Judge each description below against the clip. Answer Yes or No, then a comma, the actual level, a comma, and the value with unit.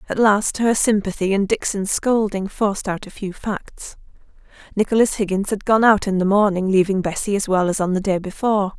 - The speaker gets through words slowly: No, average, 200 wpm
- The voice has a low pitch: No, high, 200 Hz